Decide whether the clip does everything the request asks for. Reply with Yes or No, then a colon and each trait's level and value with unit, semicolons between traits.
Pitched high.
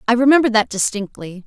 Yes: high, 230 Hz